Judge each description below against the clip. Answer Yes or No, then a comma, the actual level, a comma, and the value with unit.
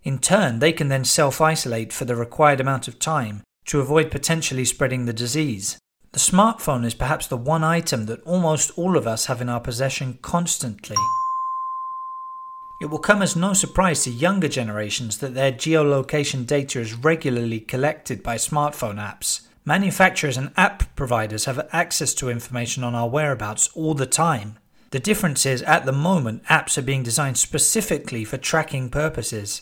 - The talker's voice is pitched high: No, medium, 140 Hz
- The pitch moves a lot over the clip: No, average, 4.7 semitones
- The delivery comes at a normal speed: Yes, average, 170 wpm